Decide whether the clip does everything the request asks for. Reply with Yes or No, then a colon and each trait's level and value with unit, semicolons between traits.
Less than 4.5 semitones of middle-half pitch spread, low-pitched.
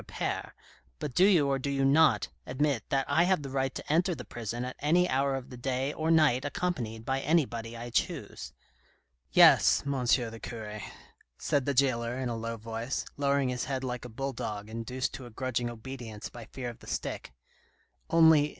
Yes: average, 3.2 semitones; low, 130 Hz